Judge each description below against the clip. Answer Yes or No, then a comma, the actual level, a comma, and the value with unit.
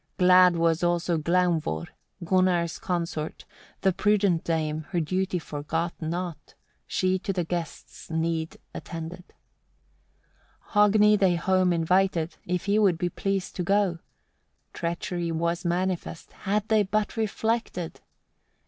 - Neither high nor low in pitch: Yes, medium, 175 Hz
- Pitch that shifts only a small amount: Yes, narrow, 2.3 semitones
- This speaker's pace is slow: Yes, slow, 120 wpm